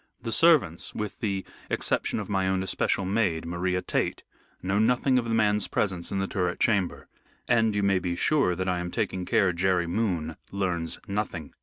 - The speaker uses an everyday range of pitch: Yes, average, 3.0 semitones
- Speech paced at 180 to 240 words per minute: Yes, average, 185 wpm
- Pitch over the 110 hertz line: No, very low, 95 Hz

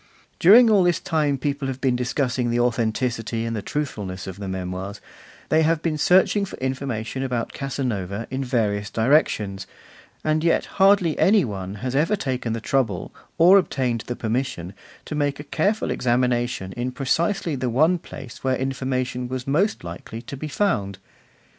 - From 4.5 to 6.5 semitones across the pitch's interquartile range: Yes, average, 5.1 semitones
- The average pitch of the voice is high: No, low, 130 Hz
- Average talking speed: Yes, average, 165 wpm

